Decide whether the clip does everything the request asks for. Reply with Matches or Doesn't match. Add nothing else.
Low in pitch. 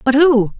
Doesn't match